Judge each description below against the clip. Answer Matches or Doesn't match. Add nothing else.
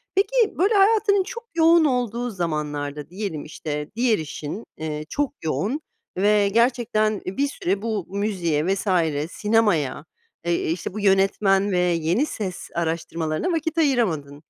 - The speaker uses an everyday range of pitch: Doesn't match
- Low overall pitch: Doesn't match